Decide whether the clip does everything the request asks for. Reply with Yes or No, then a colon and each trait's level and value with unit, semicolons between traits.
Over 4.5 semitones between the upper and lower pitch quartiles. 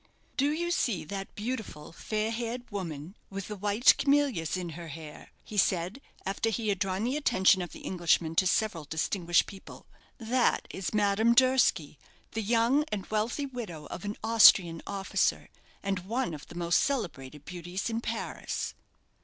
Yes: average, 5.1 semitones